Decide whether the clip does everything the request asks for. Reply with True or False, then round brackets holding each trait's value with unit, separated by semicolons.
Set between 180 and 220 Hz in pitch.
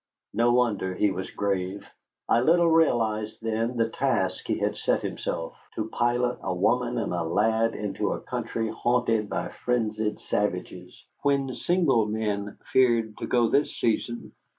False (115 Hz)